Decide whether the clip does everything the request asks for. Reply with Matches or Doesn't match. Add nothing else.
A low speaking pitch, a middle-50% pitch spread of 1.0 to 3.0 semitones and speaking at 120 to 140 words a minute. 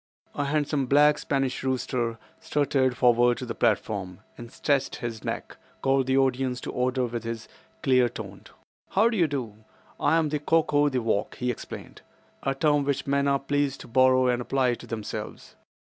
Doesn't match